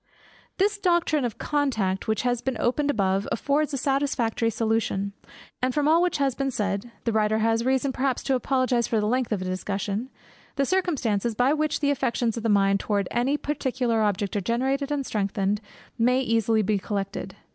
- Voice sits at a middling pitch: No, high, 240 Hz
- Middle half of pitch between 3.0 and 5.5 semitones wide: Yes, average, 4.6 semitones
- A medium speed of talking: Yes, average, 185 wpm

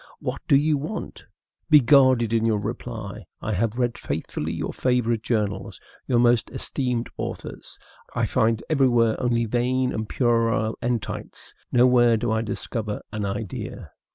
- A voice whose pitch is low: Yes, low, 120 Hz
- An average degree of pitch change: No, narrow, 2.1 semitones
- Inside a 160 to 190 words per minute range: No, average, 145 wpm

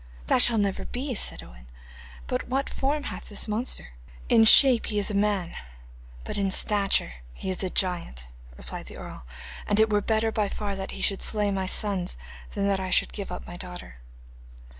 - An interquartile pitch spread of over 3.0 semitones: No, average, 2.7 semitones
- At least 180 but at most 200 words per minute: Yes, average, 195 wpm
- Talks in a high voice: Yes, high, 200 Hz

